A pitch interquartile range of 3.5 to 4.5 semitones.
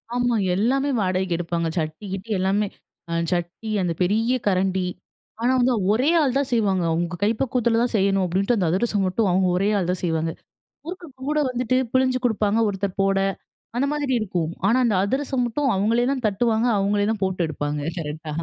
No: average, 4.9 semitones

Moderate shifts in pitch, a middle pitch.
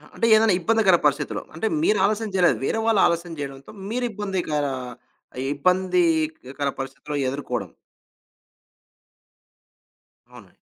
No: wide, 6.1 semitones; medium, 175 Hz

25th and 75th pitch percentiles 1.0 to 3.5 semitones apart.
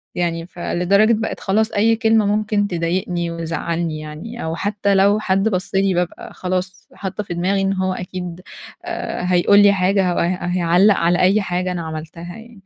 Yes: average, 2.7 semitones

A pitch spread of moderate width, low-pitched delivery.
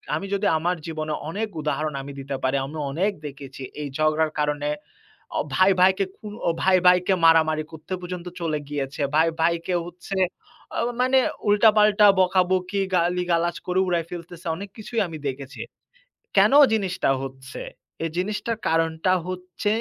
No: average, 3.3 semitones; medium, 175 Hz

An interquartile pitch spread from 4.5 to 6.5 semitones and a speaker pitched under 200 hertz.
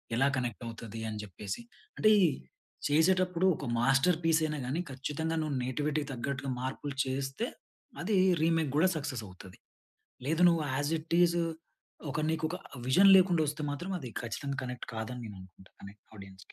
Yes: average, 4.9 semitones; medium, 140 Hz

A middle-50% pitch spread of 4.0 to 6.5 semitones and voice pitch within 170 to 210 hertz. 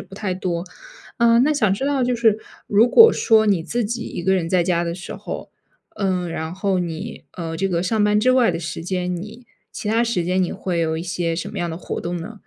Yes: average, 4.4 semitones; medium, 185 Hz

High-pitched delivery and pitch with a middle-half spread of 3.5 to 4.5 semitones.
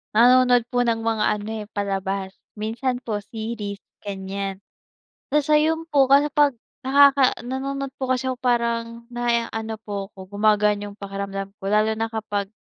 Yes: high, 225 Hz; average, 3.9 semitones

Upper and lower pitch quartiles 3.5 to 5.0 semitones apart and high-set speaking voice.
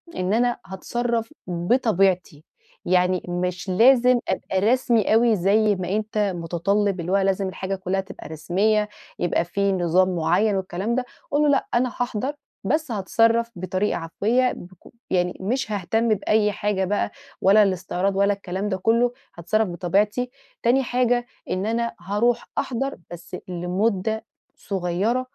Yes: average, 4.0 semitones; high, 200 Hz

